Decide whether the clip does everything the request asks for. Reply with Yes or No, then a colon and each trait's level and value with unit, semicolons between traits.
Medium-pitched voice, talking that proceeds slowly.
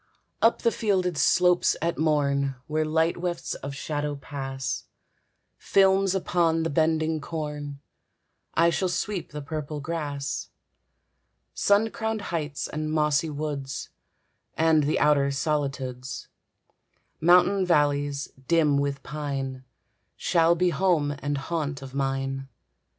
Yes: medium, 150 Hz; slow, 115 wpm